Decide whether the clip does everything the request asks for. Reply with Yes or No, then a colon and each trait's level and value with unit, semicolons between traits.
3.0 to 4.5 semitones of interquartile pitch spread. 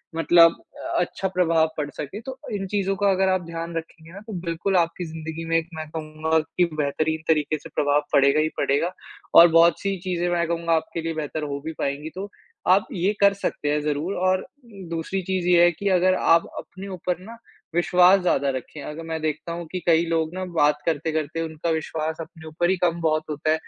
No: narrow, 2.4 semitones